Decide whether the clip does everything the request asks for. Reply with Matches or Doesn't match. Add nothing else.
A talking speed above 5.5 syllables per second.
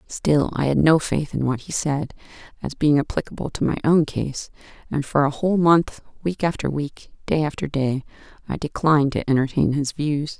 Doesn't match